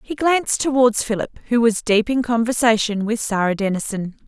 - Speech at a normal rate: Yes, average, 170 wpm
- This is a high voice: Yes, high, 230 Hz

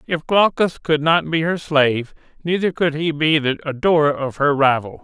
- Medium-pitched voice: Yes, medium, 150 Hz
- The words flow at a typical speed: Yes, average, 190 wpm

